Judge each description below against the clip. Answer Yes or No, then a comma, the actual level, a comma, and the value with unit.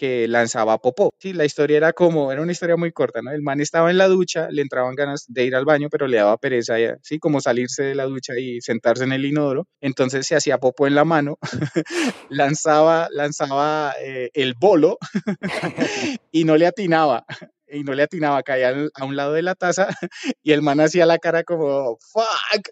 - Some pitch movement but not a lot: Yes, average, 3.7 semitones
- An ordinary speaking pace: No, fast, 210 wpm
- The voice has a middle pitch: Yes, medium, 150 Hz